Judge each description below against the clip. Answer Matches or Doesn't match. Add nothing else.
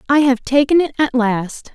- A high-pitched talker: Matches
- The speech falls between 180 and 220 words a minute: Matches